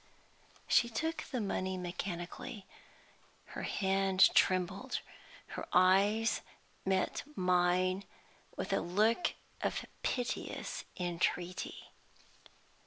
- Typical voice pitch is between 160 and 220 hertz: Yes, high, 190 Hz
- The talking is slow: Yes, slow, 85 wpm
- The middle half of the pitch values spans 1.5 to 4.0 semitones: Yes, average, 2.7 semitones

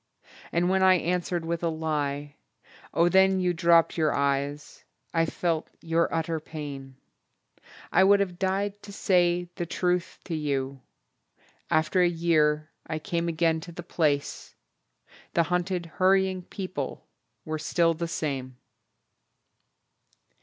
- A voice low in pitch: No, medium, 170 Hz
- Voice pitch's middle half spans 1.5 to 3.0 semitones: Yes, narrow, 2.5 semitones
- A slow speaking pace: Yes, slow, 130 wpm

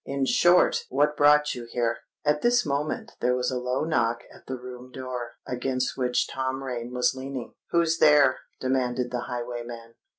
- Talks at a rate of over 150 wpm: Yes, average, 170 wpm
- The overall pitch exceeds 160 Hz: No, low, 130 Hz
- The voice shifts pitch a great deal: No, average, 2.8 semitones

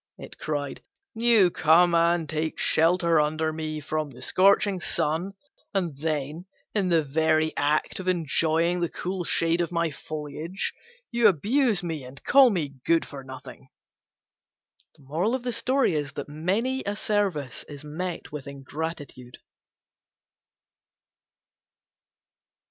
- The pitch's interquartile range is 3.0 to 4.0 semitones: Yes, average, 3.5 semitones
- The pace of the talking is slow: Yes, slow, 115 wpm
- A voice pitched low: No, medium, 165 Hz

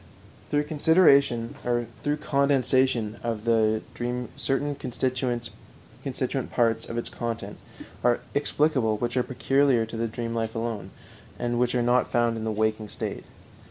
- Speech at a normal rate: No, slow, 130 wpm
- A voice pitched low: Yes, low, 120 Hz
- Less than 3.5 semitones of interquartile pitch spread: Yes, narrow, 2.5 semitones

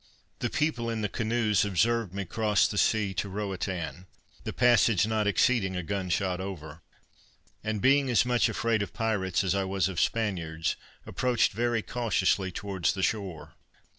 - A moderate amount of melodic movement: Yes, average, 3.4 semitones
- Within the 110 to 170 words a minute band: Yes, average, 165 wpm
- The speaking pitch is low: Yes, low, 100 Hz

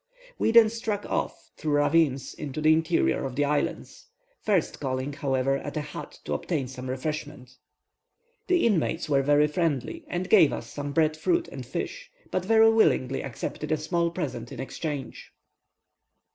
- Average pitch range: Yes, average, 4.3 semitones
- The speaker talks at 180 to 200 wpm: No, average, 160 wpm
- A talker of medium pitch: Yes, medium, 150 Hz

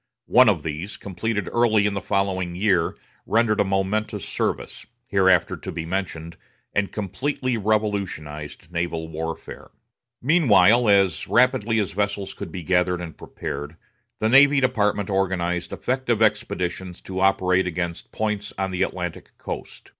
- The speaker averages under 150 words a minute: Yes, average, 140 wpm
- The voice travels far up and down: No, average, 3.4 semitones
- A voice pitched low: Yes, very low, 95 Hz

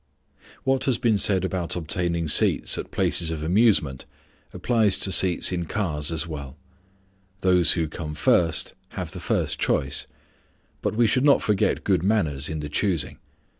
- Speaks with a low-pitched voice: Yes, very low, 85 Hz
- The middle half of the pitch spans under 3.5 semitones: No, average, 4.9 semitones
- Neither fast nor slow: Yes, average, 160 wpm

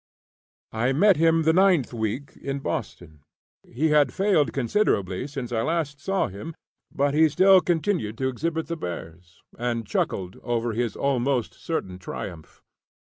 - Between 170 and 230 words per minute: No, average, 145 wpm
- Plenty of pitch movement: Yes, wide, 6.5 semitones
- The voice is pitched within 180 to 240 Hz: No, low, 135 Hz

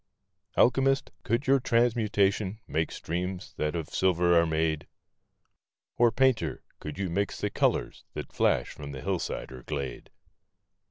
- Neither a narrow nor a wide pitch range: No, wide, 6.7 semitones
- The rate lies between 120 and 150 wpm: Yes, average, 140 wpm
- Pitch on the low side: Yes, very low, 95 Hz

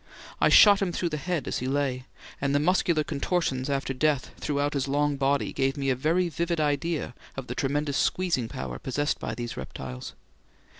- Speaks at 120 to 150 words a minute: No, average, 190 wpm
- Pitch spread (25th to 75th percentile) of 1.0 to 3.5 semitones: Yes, average, 3.0 semitones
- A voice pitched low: No, medium, 145 Hz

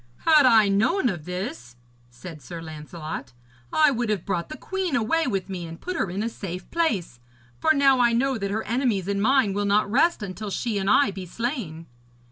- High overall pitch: Yes, high, 205 Hz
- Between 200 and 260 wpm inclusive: Yes, fast, 205 wpm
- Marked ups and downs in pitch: Yes, wide, 6.5 semitones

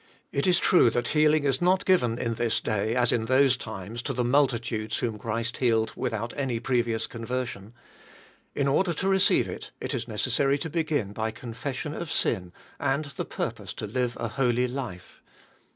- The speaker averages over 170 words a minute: Yes, average, 185 wpm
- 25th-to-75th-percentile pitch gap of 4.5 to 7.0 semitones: No, average, 3.7 semitones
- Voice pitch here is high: No, low, 125 Hz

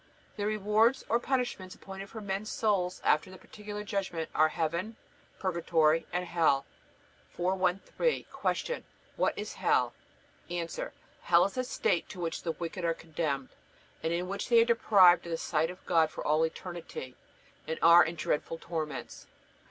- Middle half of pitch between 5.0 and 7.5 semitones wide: No, average, 3.6 semitones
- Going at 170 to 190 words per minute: No, average, 160 wpm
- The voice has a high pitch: No, medium, 175 Hz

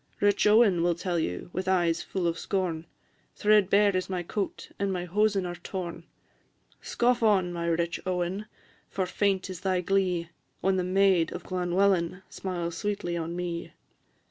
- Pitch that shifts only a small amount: Yes, narrow, 2.2 semitones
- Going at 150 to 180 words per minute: Yes, average, 160 wpm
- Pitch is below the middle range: No, medium, 185 Hz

